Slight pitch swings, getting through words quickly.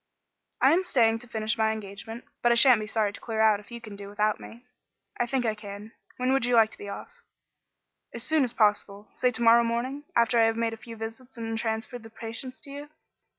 Yes: narrow, 2.0 semitones; fast, 240 wpm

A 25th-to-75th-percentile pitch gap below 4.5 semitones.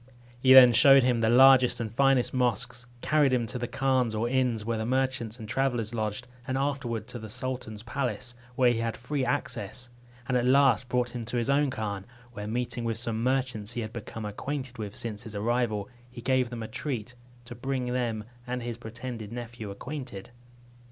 Yes: narrow, 2.5 semitones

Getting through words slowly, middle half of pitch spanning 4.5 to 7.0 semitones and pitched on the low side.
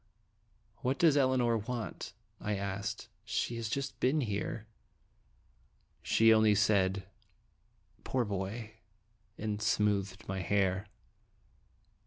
No: slow, 105 wpm; average, 2.8 semitones; low, 110 Hz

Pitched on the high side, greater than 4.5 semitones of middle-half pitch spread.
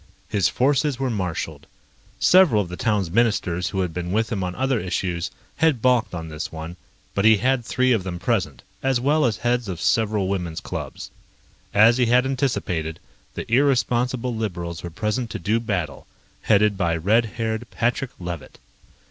No: low, 110 Hz; wide, 5.6 semitones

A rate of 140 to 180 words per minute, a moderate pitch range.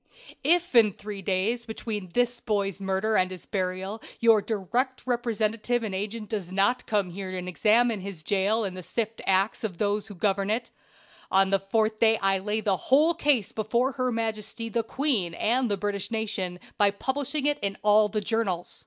No: average, 190 wpm; average, 3.0 semitones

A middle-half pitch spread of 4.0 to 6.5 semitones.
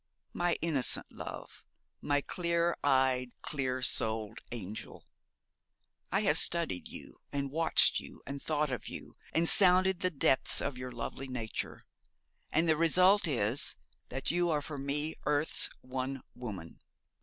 Yes: average, 4.7 semitones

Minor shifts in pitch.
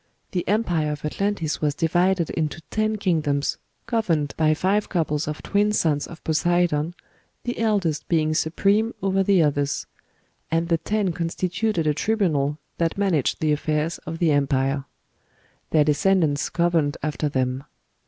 No: average, 4.3 semitones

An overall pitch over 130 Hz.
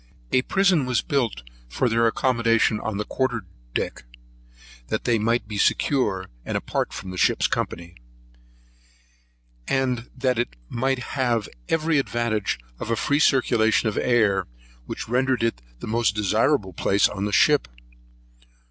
No: low, 115 Hz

